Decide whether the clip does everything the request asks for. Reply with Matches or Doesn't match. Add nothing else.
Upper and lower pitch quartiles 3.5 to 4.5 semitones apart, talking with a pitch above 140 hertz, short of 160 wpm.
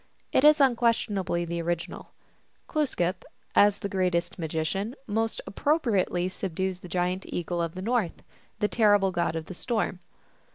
Matches